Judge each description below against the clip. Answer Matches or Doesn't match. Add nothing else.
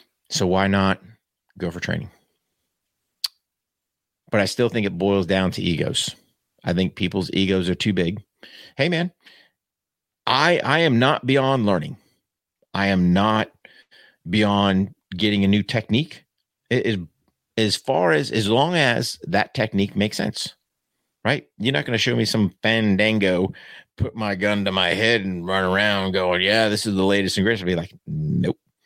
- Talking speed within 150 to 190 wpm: Matches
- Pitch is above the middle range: Doesn't match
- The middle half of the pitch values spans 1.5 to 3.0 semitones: Matches